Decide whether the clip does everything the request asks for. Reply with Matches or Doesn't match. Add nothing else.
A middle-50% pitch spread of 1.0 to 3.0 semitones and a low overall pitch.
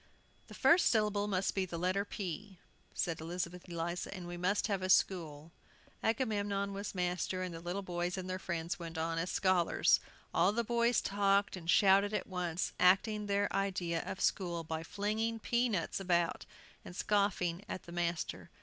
Doesn't match